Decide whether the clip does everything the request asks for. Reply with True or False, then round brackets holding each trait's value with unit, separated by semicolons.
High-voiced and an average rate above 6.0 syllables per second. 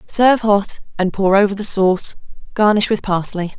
False (200 Hz; 5.2 syllables/s)